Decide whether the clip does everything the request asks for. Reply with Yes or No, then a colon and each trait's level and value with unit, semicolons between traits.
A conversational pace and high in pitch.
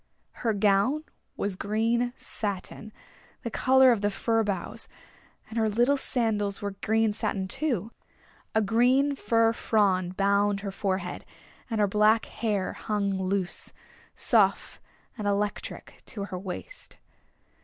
No: slow, 130 wpm; high, 210 Hz